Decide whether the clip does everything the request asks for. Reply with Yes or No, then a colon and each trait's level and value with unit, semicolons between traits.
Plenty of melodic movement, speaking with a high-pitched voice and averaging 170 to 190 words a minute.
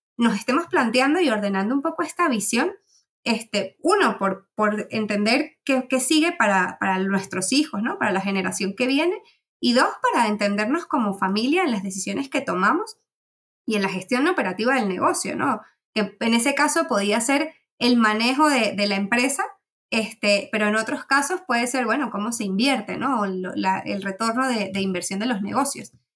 Yes: wide, 5.9 semitones; high, 235 Hz; average, 185 wpm